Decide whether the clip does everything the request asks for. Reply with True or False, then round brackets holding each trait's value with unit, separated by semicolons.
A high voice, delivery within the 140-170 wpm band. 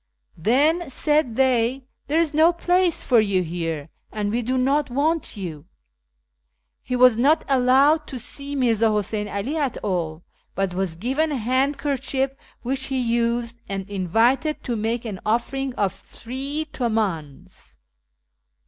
True (245 Hz; 150 wpm)